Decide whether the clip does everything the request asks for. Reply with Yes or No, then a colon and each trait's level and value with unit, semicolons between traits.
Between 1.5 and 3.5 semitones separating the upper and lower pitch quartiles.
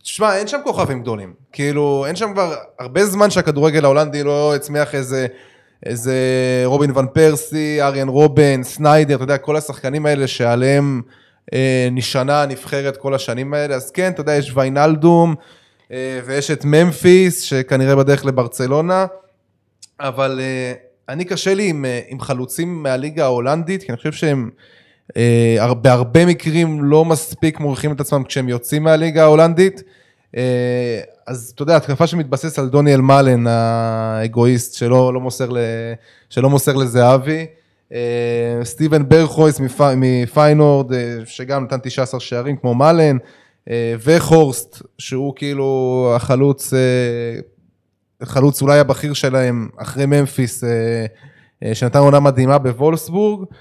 Yes: average, 3.2 semitones